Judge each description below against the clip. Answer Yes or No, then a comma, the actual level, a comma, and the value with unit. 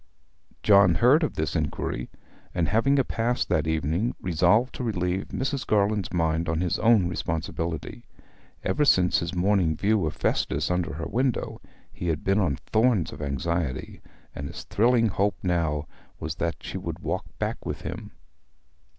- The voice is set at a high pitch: No, very low, 90 Hz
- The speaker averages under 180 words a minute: Yes, average, 160 wpm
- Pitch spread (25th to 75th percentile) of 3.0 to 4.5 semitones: No, average, 5.3 semitones